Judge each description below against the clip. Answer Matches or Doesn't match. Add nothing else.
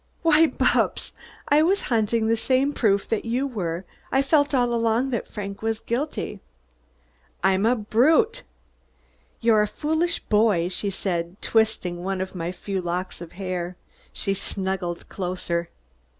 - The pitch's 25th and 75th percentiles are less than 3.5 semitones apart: Doesn't match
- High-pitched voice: Matches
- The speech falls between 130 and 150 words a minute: Matches